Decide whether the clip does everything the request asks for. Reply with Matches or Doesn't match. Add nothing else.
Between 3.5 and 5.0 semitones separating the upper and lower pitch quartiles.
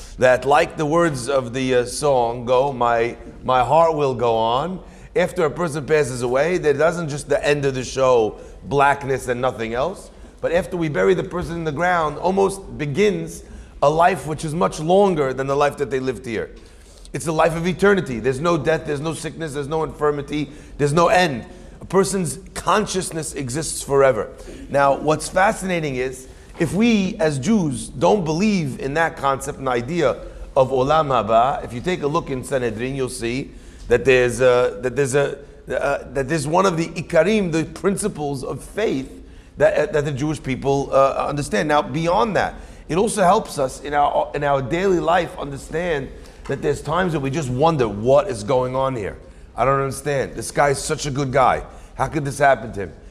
Matches